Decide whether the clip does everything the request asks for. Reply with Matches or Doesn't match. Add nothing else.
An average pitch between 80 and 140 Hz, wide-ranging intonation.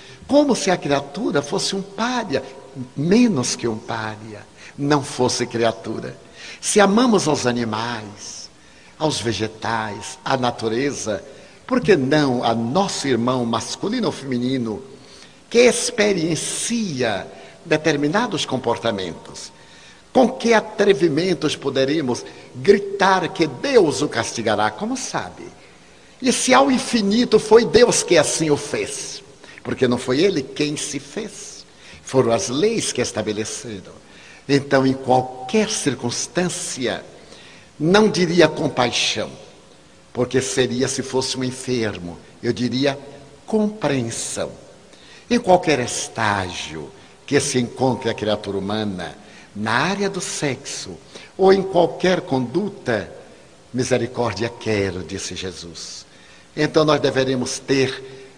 Matches